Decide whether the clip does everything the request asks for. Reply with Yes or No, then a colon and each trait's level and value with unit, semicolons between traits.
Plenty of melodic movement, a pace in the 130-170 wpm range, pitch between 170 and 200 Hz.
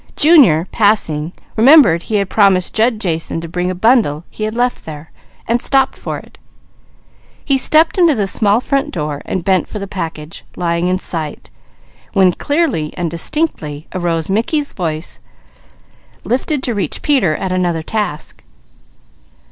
Yes: wide, 6.7 semitones; average, 150 wpm; high, 190 Hz